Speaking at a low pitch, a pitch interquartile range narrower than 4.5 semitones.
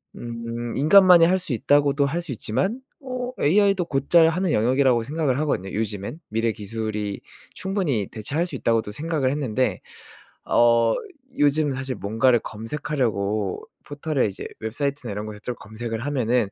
No: low, 130 Hz; wide, 5.5 semitones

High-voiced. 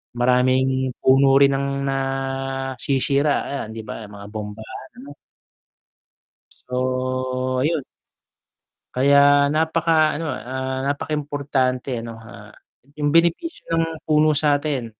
No: low, 135 Hz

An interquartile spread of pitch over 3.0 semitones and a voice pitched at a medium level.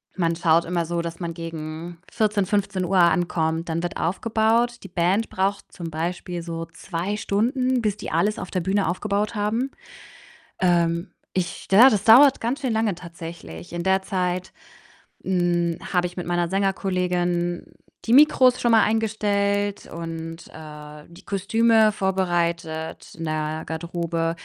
Yes: average, 3.5 semitones; medium, 180 Hz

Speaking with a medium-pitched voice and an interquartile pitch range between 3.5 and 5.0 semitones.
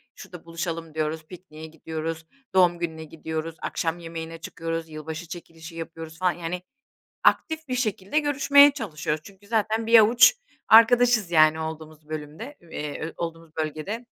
Yes: medium, 165 Hz; average, 4.7 semitones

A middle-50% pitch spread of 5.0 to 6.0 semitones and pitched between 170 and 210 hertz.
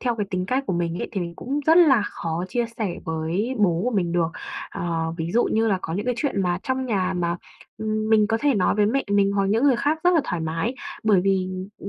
Yes: wide, 5.5 semitones; high, 200 Hz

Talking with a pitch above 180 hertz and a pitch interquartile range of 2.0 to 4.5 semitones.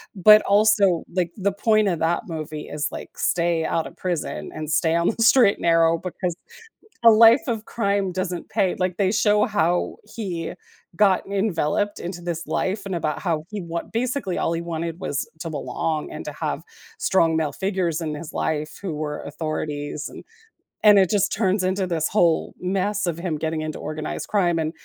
No: medium, 175 Hz; average, 3.7 semitones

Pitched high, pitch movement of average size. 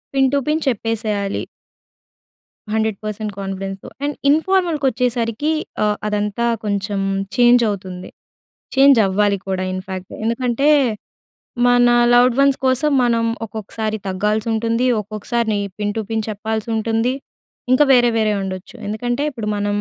Yes: high, 220 Hz; average, 3.1 semitones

